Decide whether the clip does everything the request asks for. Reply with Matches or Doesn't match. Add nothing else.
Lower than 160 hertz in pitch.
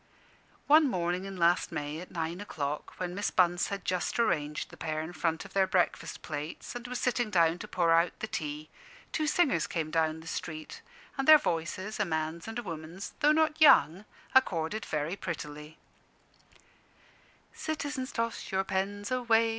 Doesn't match